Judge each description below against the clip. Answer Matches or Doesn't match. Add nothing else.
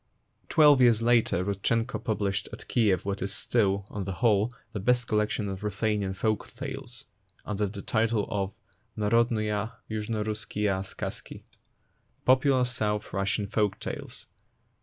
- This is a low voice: Matches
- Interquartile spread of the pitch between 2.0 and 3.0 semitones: Matches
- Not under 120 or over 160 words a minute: Matches